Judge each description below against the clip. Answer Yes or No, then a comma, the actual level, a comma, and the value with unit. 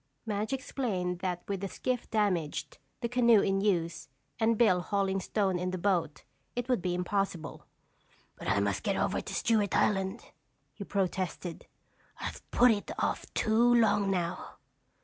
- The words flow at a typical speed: Yes, average, 155 wpm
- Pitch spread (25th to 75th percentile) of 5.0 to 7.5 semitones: No, average, 3.6 semitones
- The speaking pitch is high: Yes, high, 195 Hz